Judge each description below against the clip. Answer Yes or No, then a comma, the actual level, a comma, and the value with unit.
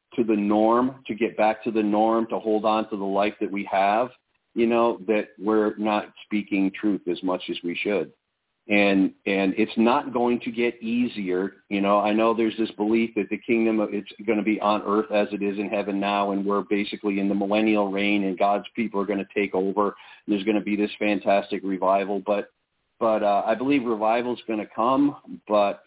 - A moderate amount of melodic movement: No, narrow, 1.8 semitones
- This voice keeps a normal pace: No, fast, 220 wpm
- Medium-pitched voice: No, low, 105 Hz